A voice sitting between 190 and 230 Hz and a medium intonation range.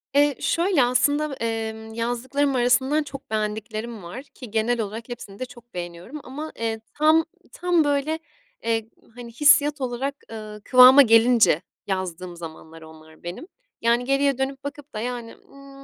No: high, 245 Hz; average, 4.1 semitones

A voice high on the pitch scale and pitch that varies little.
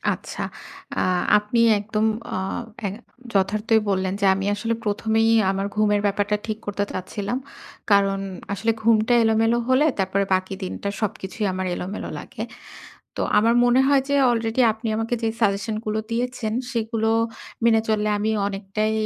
Yes: high, 215 Hz; narrow, 2.1 semitones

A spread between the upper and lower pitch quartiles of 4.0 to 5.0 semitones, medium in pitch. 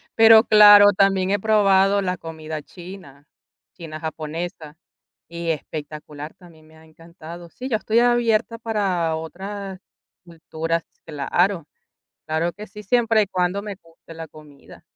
Yes: average, 4.3 semitones; medium, 175 Hz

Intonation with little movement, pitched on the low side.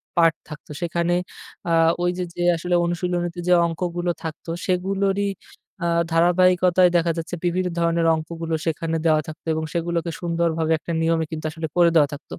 No: narrow, 1.4 semitones; medium, 170 Hz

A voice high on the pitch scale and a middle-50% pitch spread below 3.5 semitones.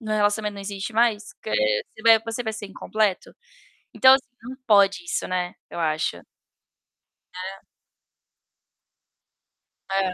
Yes: high, 210 Hz; average, 2.9 semitones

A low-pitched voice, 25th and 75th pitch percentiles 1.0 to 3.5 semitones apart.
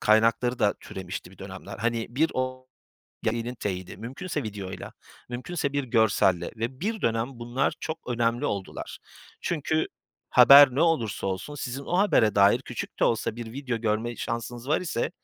No: low, 120 Hz; average, 4.0 semitones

